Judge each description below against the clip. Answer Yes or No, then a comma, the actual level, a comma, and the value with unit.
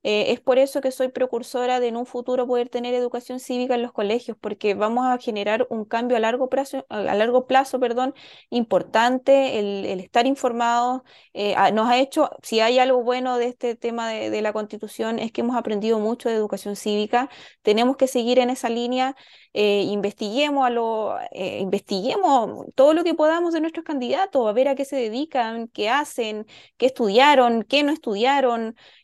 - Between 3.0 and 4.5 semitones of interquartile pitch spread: No, narrow, 2.6 semitones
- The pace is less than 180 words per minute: No, fast, 190 wpm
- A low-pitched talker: No, high, 245 Hz